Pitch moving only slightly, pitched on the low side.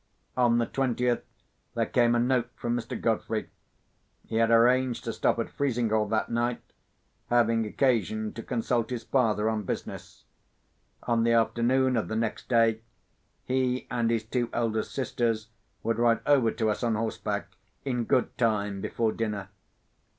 Yes: narrow, 1.7 semitones; low, 115 Hz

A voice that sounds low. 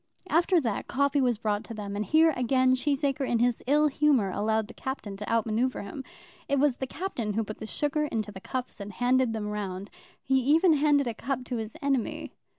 No: very high, 250 Hz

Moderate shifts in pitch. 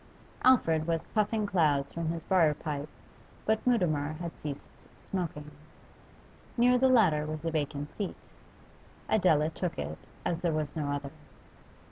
Yes: average, 4.0 semitones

